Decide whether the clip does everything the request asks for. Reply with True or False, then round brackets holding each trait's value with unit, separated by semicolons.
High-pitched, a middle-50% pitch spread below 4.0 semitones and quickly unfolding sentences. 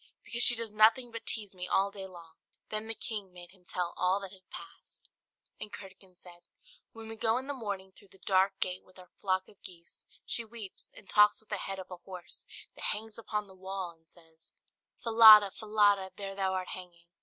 True (195 Hz; 2.7 semitones; 215 wpm)